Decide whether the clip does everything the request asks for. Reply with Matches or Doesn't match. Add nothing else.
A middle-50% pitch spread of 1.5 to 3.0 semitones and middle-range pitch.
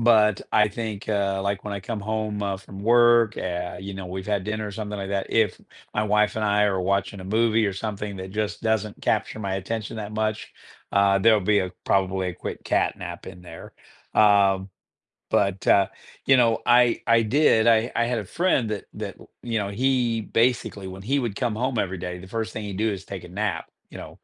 Doesn't match